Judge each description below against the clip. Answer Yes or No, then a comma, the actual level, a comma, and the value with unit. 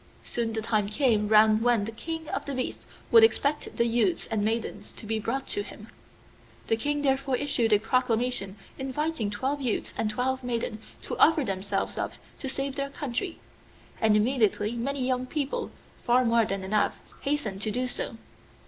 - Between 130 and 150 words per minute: No, average, 175 wpm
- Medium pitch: No, high, 240 Hz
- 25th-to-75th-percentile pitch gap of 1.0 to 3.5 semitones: No, average, 4.0 semitones